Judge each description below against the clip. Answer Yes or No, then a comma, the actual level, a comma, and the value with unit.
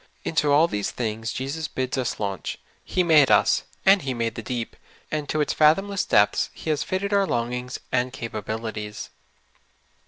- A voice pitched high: No, low, 130 Hz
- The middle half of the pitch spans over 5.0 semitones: Yes, wide, 5.6 semitones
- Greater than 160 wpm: Yes, average, 180 wpm